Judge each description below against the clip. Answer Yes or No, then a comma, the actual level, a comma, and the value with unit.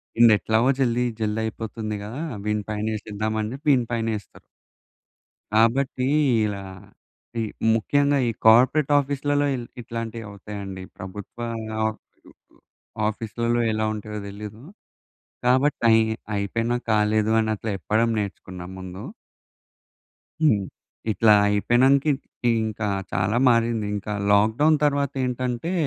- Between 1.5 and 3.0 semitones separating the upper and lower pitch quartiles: Yes, average, 2.7 semitones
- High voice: No, low, 110 Hz